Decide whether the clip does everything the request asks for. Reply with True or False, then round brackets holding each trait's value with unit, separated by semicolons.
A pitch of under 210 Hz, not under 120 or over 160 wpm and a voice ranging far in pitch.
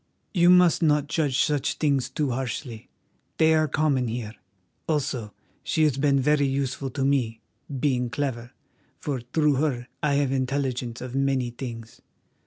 False (135 Hz; 150 wpm; 3.0 semitones)